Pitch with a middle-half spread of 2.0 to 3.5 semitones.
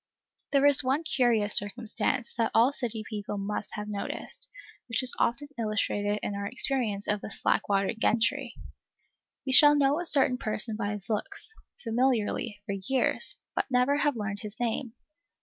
No: average, 4.1 semitones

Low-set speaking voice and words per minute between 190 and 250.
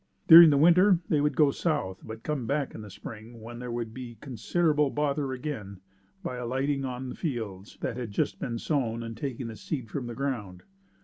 Yes: low, 125 Hz; average, 195 wpm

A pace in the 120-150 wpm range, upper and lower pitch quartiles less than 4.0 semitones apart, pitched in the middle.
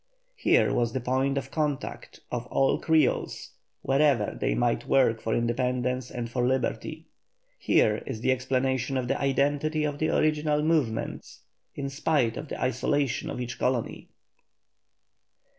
No: average, 140 wpm; average, 2.8 semitones; low, 130 Hz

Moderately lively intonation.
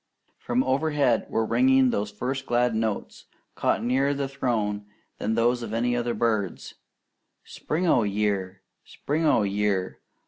Yes: average, 4.2 semitones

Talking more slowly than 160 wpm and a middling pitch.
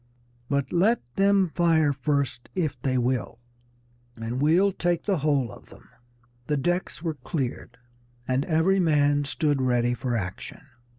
Yes: average, 140 wpm; medium, 145 Hz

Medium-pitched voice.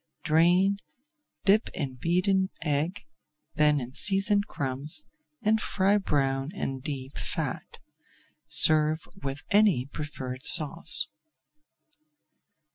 Yes: medium, 155 Hz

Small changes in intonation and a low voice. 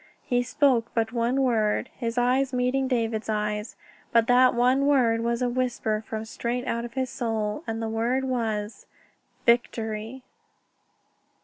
No: narrow, 2.2 semitones; high, 235 Hz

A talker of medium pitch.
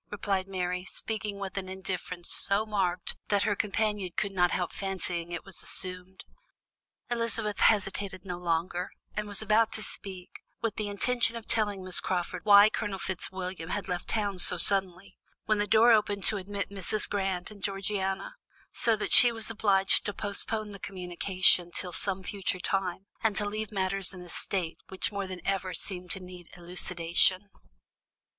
No: high, 195 Hz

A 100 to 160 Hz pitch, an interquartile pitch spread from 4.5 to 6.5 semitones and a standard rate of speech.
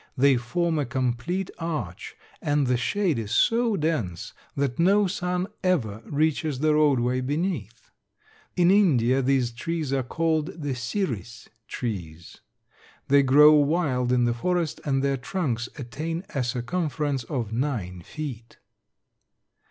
No: medium, 140 Hz; average, 5.2 semitones; slow, 130 wpm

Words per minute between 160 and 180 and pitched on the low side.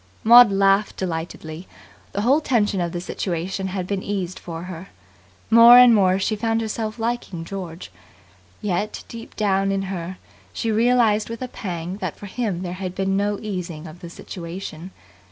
No: average, 170 wpm; high, 195 Hz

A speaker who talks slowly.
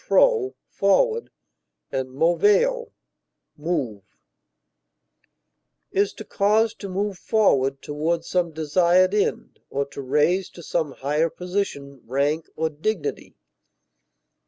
Yes: slow, 105 wpm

